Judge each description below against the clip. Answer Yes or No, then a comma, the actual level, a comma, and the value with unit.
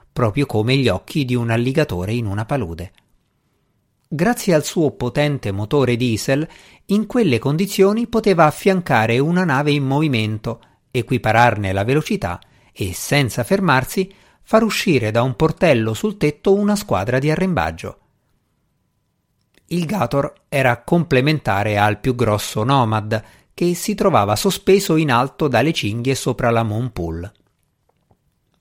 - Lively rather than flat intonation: Yes, wide, 7.3 semitones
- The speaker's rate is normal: Yes, average, 130 wpm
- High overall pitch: No, low, 135 Hz